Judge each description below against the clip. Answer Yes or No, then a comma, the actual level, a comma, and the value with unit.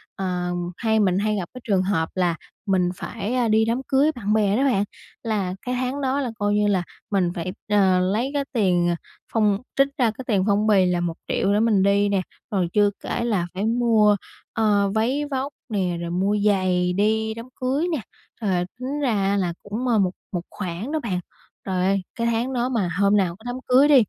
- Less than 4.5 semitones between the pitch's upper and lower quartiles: Yes, average, 4.0 semitones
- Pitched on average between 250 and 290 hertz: No, high, 210 Hz